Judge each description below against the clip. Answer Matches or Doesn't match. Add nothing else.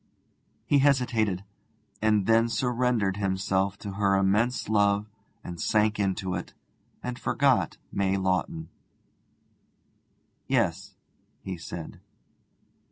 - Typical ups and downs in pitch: Matches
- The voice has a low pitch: Matches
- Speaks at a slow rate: Matches